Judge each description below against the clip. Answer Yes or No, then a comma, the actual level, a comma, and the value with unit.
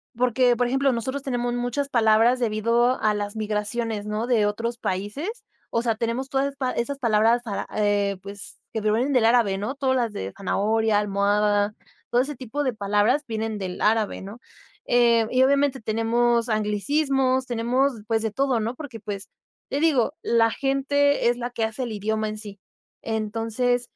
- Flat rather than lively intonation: No, average, 3.2 semitones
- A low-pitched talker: No, high, 230 Hz